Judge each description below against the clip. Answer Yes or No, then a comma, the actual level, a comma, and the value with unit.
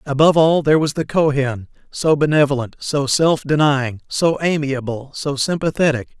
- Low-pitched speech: No, medium, 145 Hz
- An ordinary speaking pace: Yes, average, 145 wpm